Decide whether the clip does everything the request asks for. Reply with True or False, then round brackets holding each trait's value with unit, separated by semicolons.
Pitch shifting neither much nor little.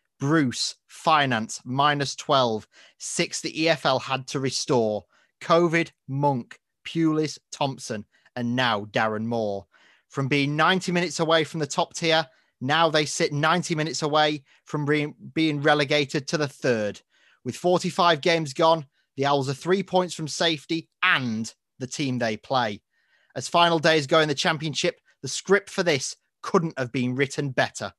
True (3.9 semitones)